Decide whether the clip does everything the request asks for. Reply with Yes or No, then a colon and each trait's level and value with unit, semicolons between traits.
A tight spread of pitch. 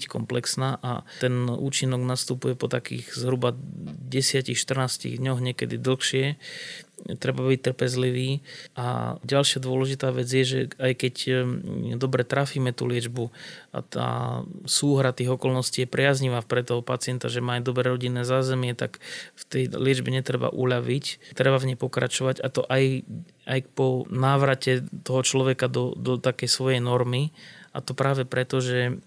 Yes: narrow, 1.0 semitones